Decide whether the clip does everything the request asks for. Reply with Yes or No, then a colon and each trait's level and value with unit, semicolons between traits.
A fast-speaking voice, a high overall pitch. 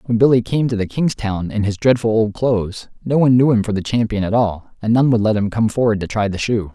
No: fast, 285 wpm; low, 110 Hz